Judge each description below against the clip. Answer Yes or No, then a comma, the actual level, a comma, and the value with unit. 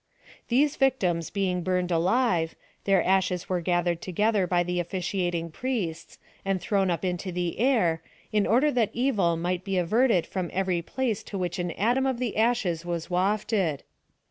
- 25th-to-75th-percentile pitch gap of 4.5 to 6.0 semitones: No, average, 4.1 semitones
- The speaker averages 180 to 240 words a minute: No, average, 165 wpm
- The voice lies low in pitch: No, medium, 185 Hz